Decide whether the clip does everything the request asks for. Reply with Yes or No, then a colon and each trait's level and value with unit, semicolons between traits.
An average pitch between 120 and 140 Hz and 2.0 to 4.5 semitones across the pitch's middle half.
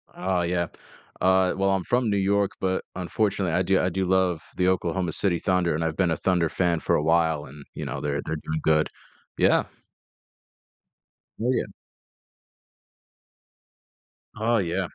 No: very low, 90 Hz; narrow, 2.5 semitones